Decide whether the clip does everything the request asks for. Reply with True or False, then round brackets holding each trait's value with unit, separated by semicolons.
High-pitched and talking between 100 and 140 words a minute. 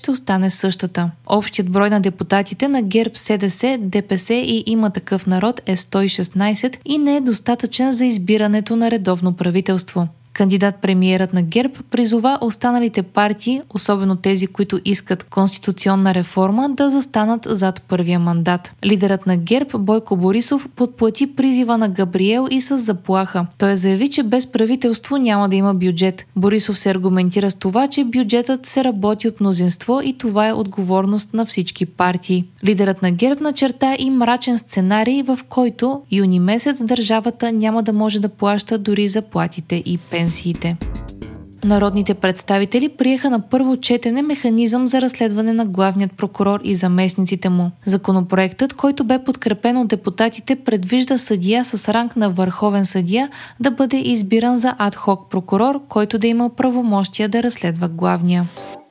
False (210 Hz; 150 wpm)